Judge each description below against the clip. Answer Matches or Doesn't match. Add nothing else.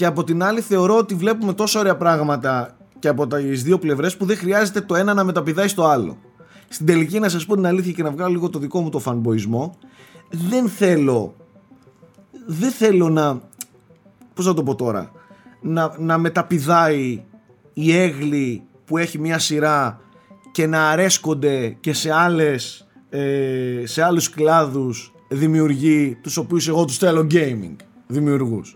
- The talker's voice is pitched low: Doesn't match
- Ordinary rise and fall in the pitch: Matches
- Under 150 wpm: Doesn't match